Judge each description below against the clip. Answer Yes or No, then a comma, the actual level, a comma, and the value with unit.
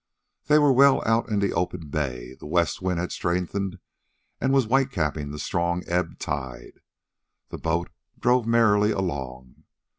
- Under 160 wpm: Yes, average, 150 wpm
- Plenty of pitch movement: Yes, wide, 6.8 semitones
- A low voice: Yes, very low, 90 Hz